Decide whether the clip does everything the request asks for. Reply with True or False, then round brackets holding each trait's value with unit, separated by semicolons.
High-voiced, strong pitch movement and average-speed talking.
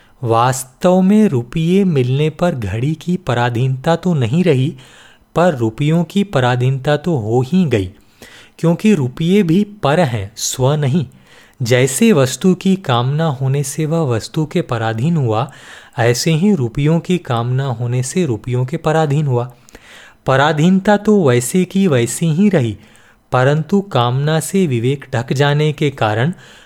False (145 Hz; 5.8 semitones; 140 wpm)